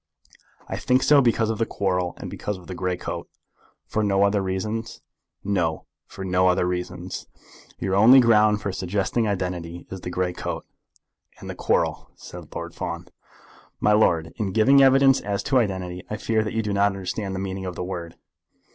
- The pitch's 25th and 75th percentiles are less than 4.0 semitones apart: Yes, average, 3.0 semitones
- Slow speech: No, average, 185 wpm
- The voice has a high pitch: No, low, 100 Hz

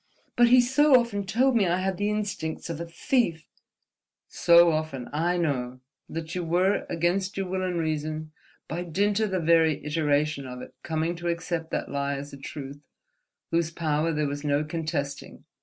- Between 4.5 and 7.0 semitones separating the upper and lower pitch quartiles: No, average, 3.7 semitones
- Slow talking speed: No, average, 175 wpm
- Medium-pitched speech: Yes, medium, 165 Hz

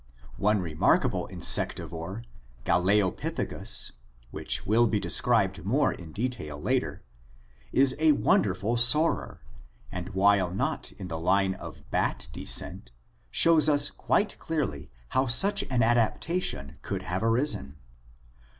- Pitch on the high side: No, low, 105 Hz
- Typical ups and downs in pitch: No, wide, 6.1 semitones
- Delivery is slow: Yes, slow, 115 wpm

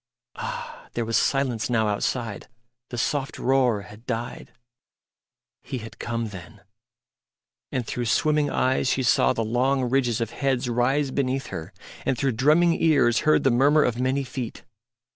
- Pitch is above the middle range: No, low, 125 Hz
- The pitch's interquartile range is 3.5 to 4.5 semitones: No, average, 2.8 semitones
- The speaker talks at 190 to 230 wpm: No, average, 155 wpm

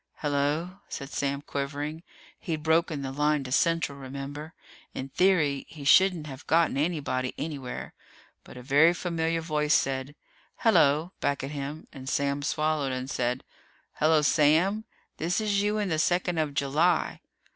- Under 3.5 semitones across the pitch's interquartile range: Yes, average, 3.0 semitones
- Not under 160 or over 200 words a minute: No, average, 150 wpm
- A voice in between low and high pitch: Yes, medium, 150 Hz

